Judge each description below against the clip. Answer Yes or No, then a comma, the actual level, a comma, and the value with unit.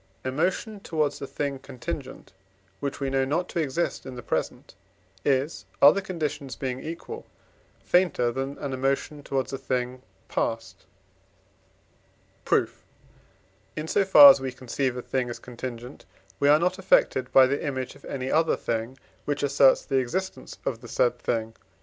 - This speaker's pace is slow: No, average, 160 wpm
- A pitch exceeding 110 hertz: Yes, low, 135 Hz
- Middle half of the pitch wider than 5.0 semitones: No, average, 3.3 semitones